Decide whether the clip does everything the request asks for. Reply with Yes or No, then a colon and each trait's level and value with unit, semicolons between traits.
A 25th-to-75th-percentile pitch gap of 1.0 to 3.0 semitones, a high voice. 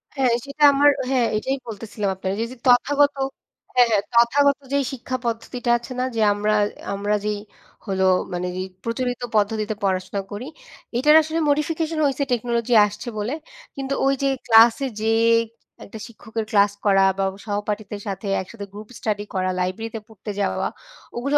No: average, 4.0 semitones; high, 225 Hz